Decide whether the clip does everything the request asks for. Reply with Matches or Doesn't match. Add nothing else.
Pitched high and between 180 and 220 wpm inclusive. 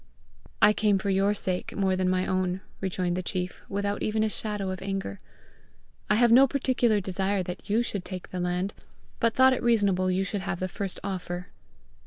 Matches